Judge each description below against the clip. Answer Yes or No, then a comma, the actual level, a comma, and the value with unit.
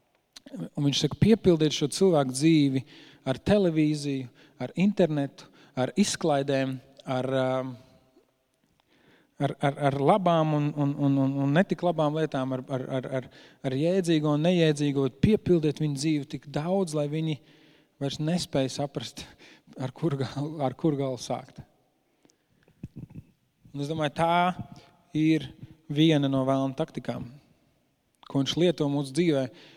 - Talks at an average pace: No, slow, 125 wpm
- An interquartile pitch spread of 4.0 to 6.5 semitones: No, average, 2.8 semitones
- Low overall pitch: No, medium, 145 Hz